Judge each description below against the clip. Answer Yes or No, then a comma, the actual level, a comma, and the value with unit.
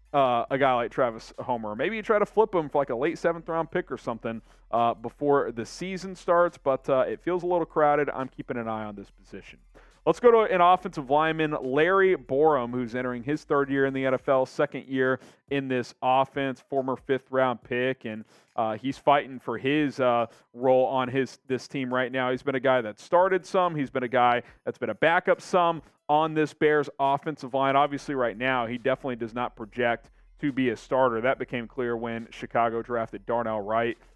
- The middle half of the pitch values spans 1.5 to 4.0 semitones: Yes, average, 3.5 semitones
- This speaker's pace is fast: Yes, fast, 210 wpm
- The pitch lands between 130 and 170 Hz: Yes, low, 135 Hz